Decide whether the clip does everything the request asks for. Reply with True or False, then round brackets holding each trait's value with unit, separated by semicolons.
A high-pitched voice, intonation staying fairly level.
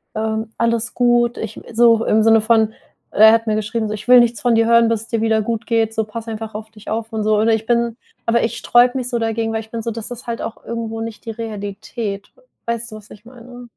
True (225 Hz; 1.1 semitones)